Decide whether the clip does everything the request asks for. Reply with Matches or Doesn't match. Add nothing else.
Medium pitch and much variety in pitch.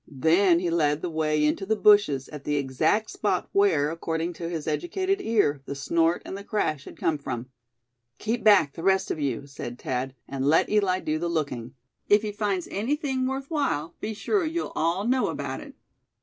Matches